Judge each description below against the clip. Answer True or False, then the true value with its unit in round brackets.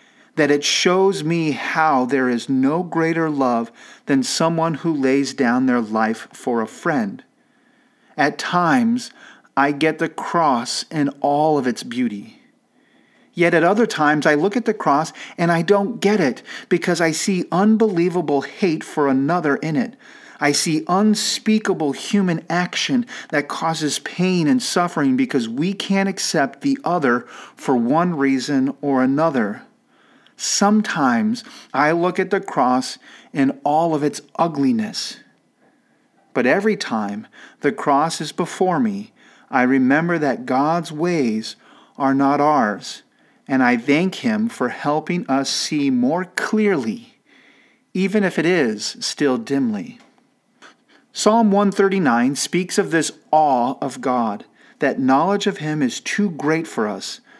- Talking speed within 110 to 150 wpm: True (140 wpm)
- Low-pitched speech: False (170 Hz)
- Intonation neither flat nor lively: False (6.8 semitones)